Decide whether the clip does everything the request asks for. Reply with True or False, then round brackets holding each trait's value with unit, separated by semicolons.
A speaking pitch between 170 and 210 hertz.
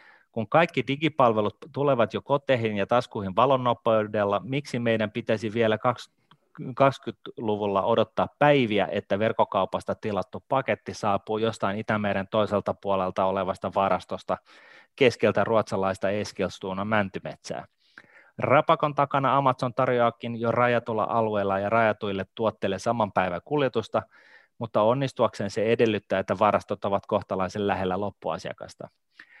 False (110 Hz)